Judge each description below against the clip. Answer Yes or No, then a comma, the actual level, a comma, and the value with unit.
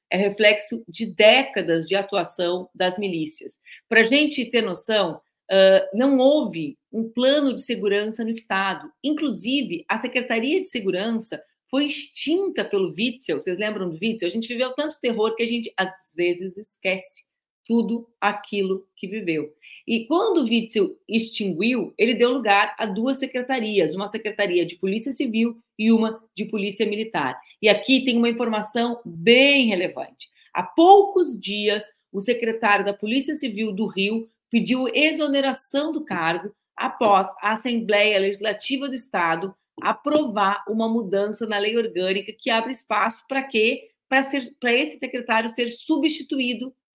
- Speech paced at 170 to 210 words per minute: No, average, 145 wpm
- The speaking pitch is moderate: No, high, 225 Hz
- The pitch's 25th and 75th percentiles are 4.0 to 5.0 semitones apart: Yes, average, 4.3 semitones